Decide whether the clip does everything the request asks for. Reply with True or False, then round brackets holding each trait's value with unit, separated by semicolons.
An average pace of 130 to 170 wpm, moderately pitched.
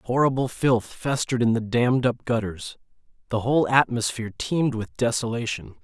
False (145 wpm; 120 Hz)